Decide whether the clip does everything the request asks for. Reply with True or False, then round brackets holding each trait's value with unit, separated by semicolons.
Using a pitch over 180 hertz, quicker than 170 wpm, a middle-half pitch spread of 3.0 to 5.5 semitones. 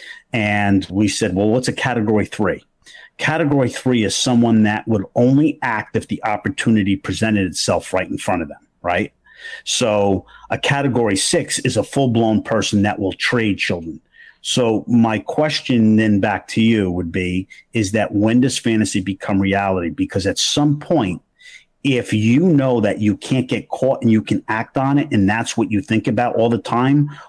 False (110 Hz; 180 wpm; 4.1 semitones)